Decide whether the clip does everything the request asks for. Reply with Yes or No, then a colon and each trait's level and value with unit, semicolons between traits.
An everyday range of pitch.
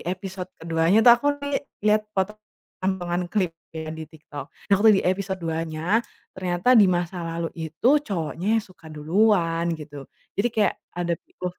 Yes: average, 3.5 semitones